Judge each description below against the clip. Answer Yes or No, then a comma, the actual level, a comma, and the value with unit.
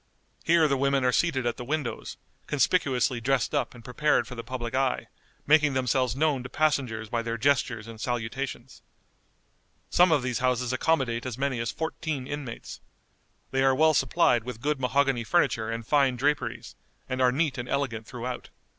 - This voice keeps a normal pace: Yes, average, 170 wpm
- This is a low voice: Yes, low, 130 Hz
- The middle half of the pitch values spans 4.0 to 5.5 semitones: No, average, 2.8 semitones